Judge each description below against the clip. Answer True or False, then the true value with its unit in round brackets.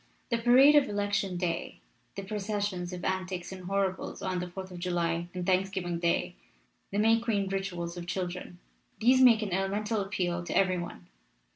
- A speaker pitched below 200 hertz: True (190 Hz)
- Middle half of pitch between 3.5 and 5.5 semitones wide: False (2.6 semitones)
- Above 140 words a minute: True (170 wpm)